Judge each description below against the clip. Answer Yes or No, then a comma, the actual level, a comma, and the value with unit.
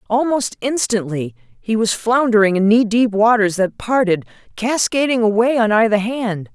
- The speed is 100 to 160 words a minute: Yes, average, 145 wpm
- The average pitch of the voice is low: No, high, 220 Hz